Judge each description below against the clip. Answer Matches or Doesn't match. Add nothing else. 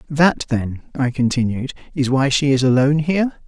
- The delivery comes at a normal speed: Matches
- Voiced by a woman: Doesn't match